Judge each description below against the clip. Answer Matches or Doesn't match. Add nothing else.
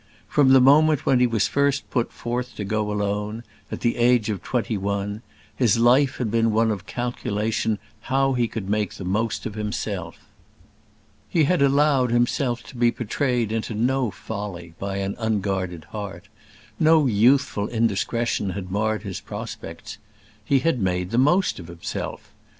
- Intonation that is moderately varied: Matches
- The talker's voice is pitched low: Matches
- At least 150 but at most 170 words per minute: Matches